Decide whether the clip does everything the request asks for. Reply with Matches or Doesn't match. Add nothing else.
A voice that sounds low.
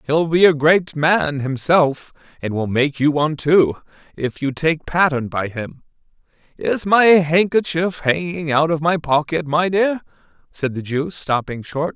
Doesn't match